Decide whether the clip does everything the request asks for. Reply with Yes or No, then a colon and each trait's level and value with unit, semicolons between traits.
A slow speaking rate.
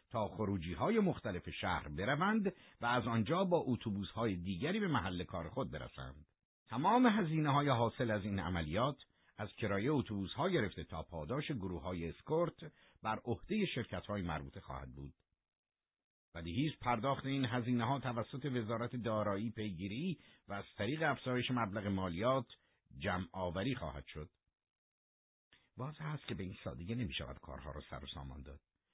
No: fast, 155 wpm